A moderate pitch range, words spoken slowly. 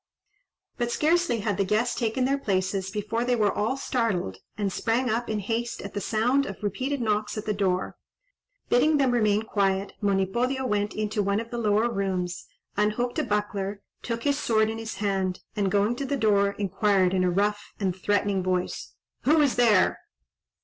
No: average, 3.2 semitones; average, 185 wpm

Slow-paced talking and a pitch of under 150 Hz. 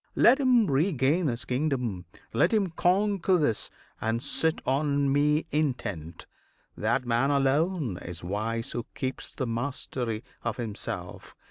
Yes: slow, 130 wpm; low, 135 Hz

